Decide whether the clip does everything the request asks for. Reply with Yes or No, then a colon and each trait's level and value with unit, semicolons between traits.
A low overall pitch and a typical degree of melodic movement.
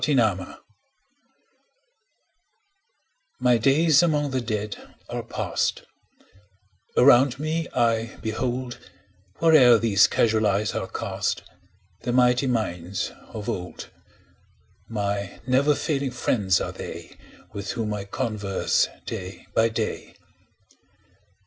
Yes: low, 115 Hz; average, 4.0 semitones